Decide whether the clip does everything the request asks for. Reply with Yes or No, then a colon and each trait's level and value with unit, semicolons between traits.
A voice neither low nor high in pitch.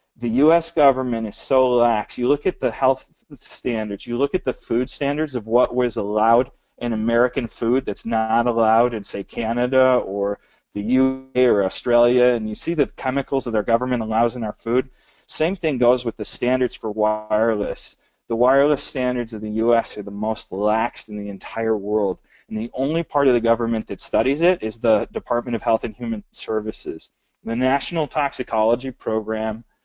No: low, 120 Hz